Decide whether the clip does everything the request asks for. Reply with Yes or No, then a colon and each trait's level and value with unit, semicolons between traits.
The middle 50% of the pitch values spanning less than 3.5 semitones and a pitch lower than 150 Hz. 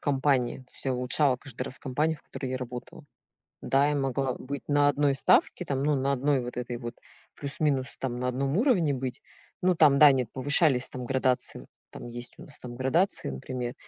Yes: narrow, 2.4 semitones; low, 135 Hz